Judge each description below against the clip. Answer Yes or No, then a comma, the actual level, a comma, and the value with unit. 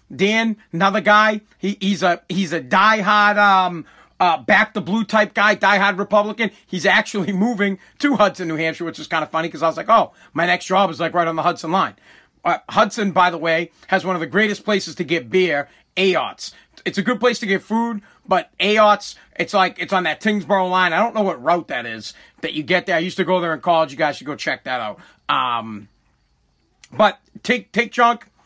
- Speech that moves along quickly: Yes, fast, 225 wpm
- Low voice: No, high, 190 Hz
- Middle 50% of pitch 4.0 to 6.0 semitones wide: No, average, 3.6 semitones